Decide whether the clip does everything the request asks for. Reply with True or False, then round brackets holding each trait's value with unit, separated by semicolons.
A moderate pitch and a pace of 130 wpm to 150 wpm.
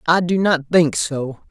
False (150 Hz; 200 wpm)